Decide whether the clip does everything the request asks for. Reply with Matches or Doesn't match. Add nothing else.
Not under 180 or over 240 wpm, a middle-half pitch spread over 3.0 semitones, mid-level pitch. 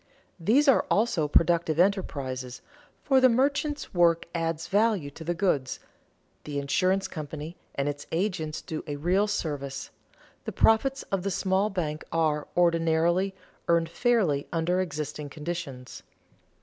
Doesn't match